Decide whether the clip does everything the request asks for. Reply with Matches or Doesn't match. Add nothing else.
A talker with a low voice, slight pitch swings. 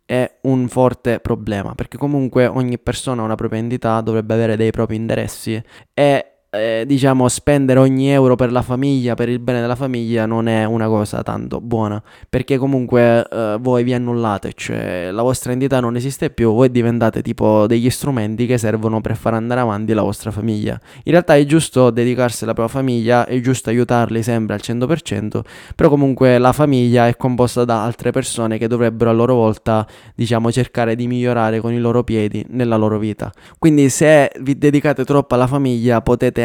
Matches